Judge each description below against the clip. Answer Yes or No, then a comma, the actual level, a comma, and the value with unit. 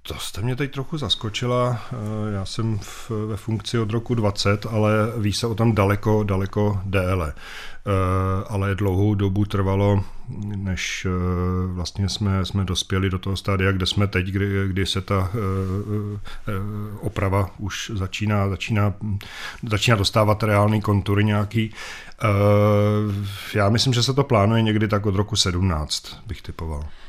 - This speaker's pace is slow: No, average, 150 wpm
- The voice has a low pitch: Yes, low, 100 Hz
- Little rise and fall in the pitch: Yes, narrow, 1.8 semitones